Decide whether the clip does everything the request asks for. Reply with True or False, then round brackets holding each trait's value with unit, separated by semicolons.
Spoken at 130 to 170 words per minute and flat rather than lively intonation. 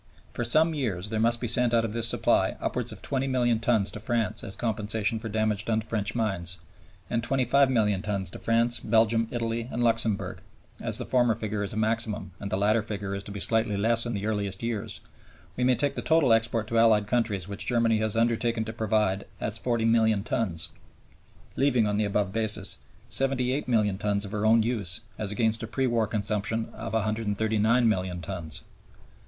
False (190 wpm; 2.2 semitones)